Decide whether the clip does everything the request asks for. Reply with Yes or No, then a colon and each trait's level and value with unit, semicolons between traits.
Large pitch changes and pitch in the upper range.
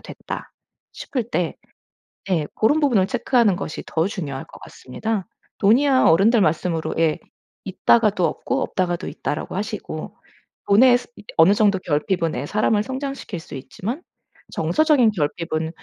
Yes: wide, 6.1 semitones; high, 195 Hz